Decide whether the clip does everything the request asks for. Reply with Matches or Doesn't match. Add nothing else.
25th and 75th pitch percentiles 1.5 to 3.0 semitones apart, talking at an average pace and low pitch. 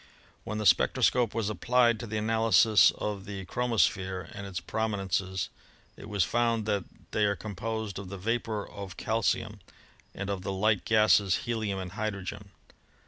Matches